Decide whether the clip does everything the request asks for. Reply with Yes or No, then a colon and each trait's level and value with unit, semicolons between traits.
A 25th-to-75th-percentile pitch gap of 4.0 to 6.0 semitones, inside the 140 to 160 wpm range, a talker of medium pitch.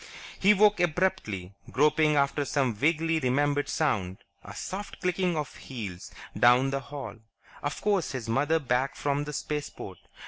Yes: average, 4.3 semitones; average, 145 wpm; medium, 145 Hz